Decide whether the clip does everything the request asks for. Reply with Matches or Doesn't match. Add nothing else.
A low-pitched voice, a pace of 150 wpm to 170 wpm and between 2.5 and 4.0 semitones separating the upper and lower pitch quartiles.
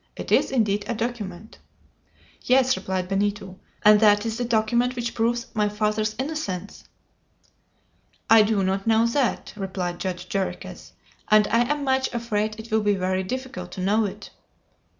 Doesn't match